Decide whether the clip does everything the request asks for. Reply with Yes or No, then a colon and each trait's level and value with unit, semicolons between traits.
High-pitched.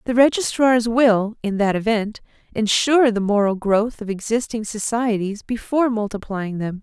Yes: high, 220 Hz